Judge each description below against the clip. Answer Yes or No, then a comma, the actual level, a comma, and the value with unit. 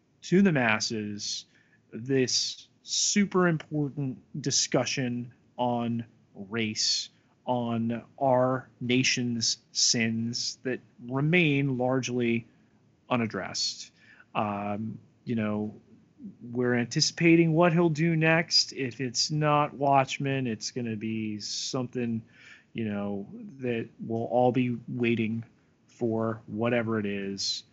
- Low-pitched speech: Yes, low, 120 Hz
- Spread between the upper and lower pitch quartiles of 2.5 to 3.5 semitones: Yes, average, 3.0 semitones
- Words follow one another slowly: Yes, slow, 100 wpm